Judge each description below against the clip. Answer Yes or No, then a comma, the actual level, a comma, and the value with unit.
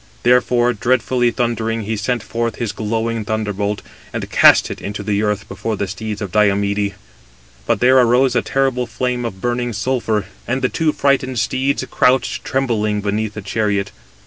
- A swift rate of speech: No, average, 165 wpm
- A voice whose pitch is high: No, low, 115 Hz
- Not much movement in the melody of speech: No, average, 3.0 semitones